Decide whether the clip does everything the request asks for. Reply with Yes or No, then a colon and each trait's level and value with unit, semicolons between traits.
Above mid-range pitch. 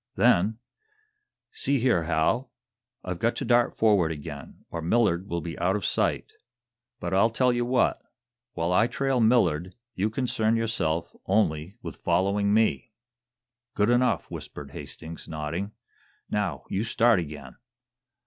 No: low, 100 Hz